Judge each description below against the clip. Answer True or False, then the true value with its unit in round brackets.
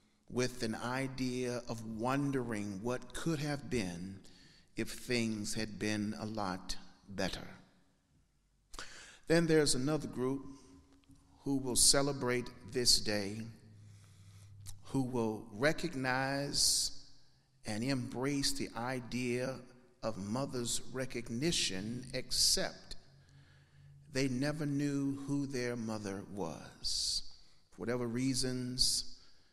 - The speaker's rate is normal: False (95 wpm)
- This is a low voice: True (125 Hz)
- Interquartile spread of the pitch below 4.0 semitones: False (4.4 semitones)